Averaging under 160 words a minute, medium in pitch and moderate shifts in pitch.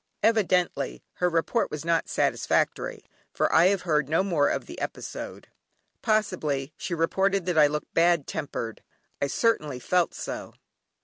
Yes: average, 145 wpm; medium, 170 Hz; average, 3.9 semitones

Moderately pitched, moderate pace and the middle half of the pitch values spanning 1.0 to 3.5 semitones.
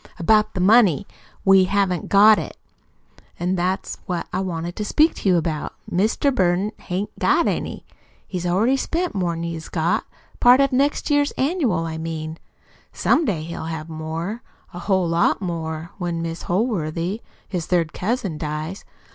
No: medium, 180 Hz; average, 160 wpm; average, 4.1 semitones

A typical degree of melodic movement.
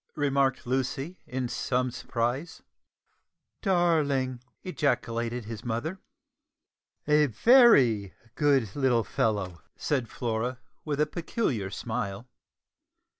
Yes: average, 4.3 semitones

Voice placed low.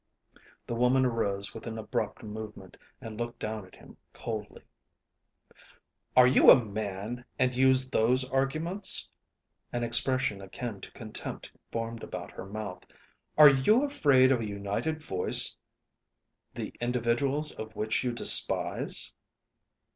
Yes: low, 120 Hz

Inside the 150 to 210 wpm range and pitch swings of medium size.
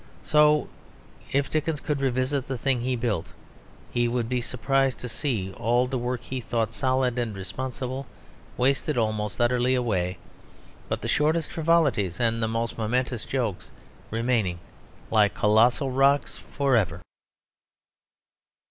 No: slow, 135 wpm; average, 3.1 semitones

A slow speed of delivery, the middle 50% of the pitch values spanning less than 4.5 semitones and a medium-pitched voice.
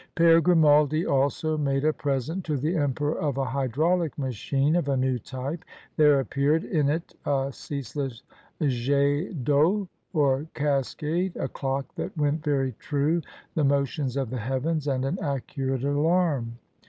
No: average, 150 wpm; narrow, 2.6 semitones; medium, 145 Hz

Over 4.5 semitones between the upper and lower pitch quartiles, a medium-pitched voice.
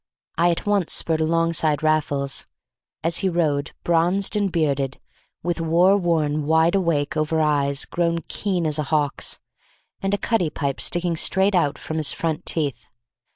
No: narrow, 2.6 semitones; medium, 165 Hz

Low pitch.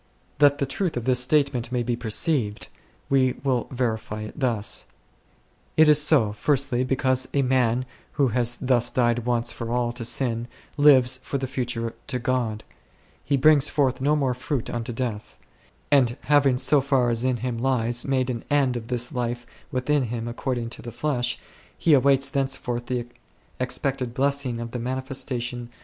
Yes: low, 125 Hz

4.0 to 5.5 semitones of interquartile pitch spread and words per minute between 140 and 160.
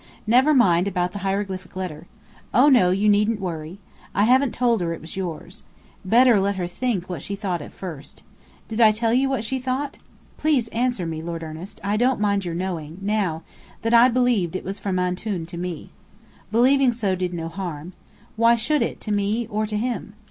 No: average, 4.8 semitones; average, 200 wpm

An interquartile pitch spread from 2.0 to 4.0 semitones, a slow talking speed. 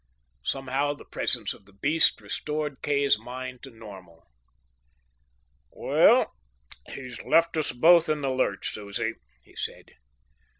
No: average, 4.9 semitones; slow, 125 wpm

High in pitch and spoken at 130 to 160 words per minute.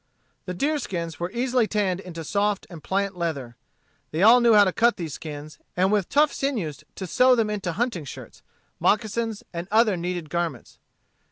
No: high, 195 Hz; average, 175 wpm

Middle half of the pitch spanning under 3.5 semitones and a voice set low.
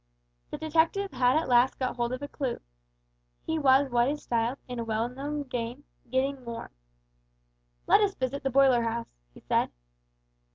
No: average, 3.1 semitones; very high, 260 Hz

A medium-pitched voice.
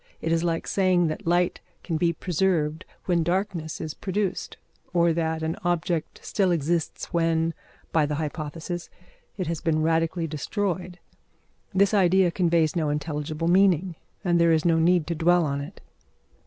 Yes: medium, 170 Hz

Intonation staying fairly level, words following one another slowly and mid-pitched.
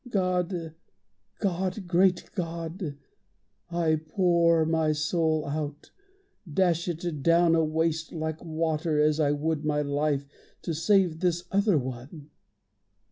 Yes: narrow, 2.3 semitones; slow, 115 wpm; medium, 165 Hz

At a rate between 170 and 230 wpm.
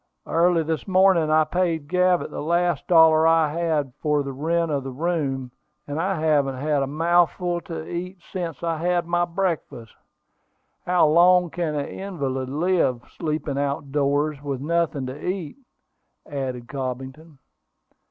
No: average, 150 wpm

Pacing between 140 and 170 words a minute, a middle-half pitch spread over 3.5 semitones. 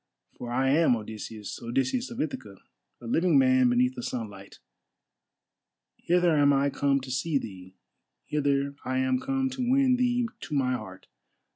Yes: average, 155 wpm; average, 5.2 semitones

